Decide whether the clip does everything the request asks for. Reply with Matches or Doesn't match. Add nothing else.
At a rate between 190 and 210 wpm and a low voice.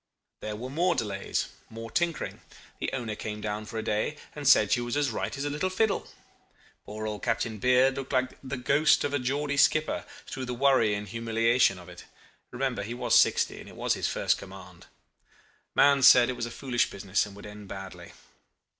Matches